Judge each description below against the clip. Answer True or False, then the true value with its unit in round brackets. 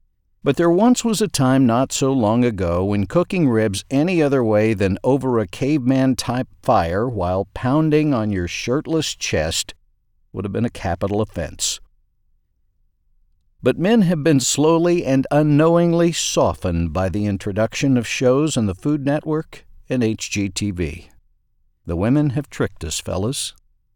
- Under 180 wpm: True (145 wpm)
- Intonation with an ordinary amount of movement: False (7.1 semitones)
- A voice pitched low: True (120 Hz)